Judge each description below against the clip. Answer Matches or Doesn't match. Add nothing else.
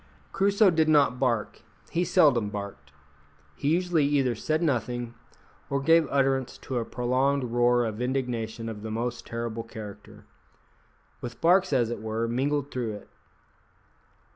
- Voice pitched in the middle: Doesn't match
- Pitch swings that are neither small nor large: Matches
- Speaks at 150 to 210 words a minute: Doesn't match